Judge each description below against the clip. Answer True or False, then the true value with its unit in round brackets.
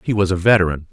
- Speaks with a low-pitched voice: True (95 Hz)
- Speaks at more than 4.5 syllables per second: True (7.5 syllables/s)